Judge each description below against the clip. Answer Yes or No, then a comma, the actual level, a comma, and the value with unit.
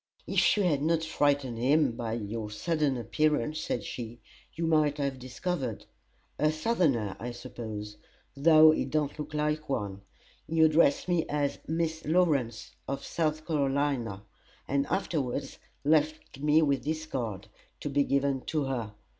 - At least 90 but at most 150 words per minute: Yes, average, 145 wpm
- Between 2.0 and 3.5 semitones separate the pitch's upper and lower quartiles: No, average, 4.3 semitones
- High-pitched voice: No, medium, 145 Hz